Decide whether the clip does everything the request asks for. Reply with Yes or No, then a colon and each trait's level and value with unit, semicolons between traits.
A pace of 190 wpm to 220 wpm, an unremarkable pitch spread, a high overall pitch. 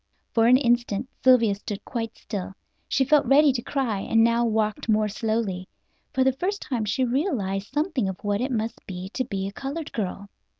Yes: average, 195 wpm; average, 4.4 semitones; high, 230 Hz